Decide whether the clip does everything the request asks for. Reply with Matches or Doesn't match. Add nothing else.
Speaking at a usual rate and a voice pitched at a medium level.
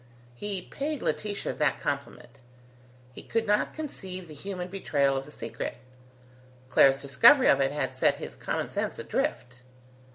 Matches